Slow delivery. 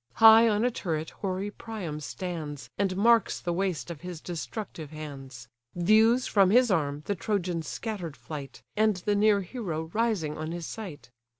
No: average, 165 wpm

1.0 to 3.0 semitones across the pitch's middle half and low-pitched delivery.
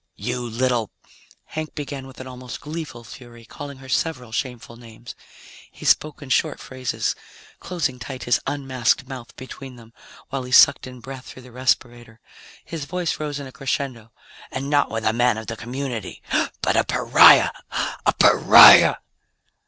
Yes: average, 2.7 semitones; low, 130 Hz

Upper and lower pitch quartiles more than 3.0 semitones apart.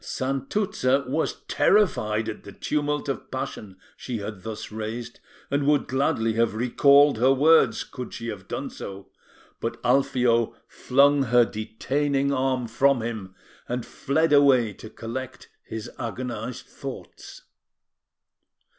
Yes: average, 3.8 semitones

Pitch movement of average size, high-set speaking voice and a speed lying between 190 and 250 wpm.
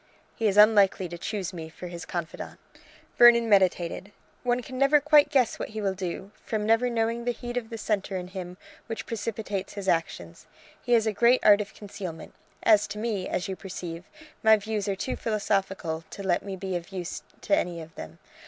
Yes: average, 3.7 semitones; high, 205 Hz; average, 200 wpm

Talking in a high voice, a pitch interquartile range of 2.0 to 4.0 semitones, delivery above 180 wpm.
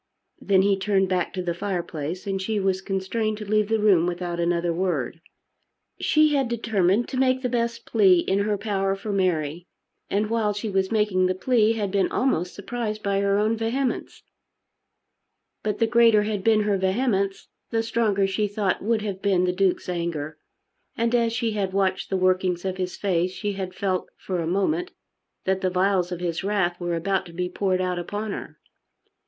Yes: high, 195 Hz; average, 2.8 semitones; average, 190 wpm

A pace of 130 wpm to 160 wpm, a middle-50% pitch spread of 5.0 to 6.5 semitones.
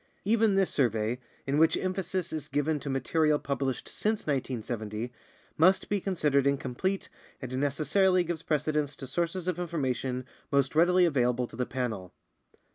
Yes: average, 145 wpm; wide, 5.4 semitones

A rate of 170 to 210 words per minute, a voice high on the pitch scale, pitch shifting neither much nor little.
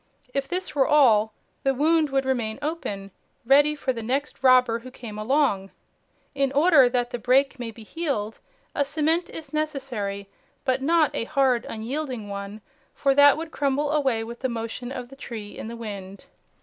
Yes: average, 175 wpm; very high, 260 Hz; average, 4.1 semitones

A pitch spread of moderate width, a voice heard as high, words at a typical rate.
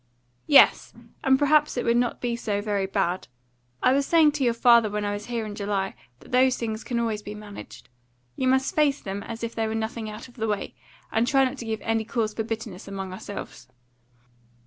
No: average, 3.3 semitones; high, 225 Hz; fast, 215 wpm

